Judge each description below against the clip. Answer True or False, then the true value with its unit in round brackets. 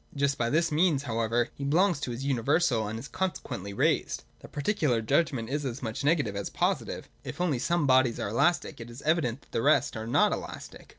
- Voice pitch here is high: False (135 Hz)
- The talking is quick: True (215 wpm)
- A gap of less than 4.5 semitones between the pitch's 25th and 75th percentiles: False (4.8 semitones)